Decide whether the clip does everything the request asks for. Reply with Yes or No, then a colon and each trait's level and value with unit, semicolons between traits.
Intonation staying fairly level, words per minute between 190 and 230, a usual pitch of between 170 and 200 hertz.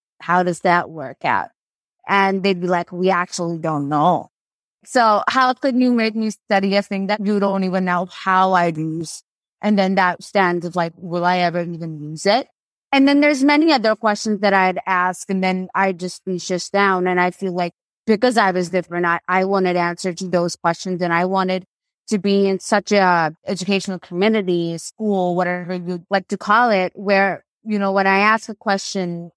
Yes: narrow, 2.3 semitones; average, 200 wpm; medium, 185 Hz